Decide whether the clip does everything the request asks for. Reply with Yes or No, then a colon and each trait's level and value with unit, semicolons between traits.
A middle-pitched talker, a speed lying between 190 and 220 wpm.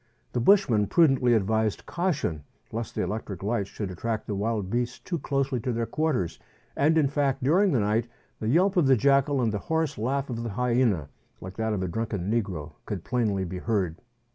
No: low, 115 Hz; average, 195 wpm